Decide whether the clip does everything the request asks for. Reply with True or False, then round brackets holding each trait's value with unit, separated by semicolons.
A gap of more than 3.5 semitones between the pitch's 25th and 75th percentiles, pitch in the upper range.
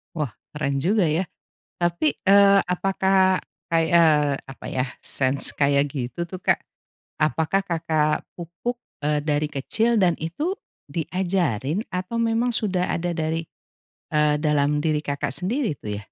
False (4.2 semitones; 165 Hz)